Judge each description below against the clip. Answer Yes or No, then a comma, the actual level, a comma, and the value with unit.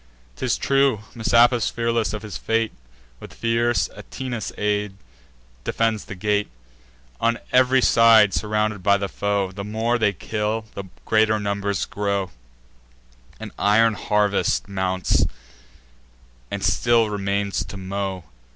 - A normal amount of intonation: No, narrow, 2.2 semitones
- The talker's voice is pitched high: No, low, 105 Hz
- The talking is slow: Yes, slow, 125 wpm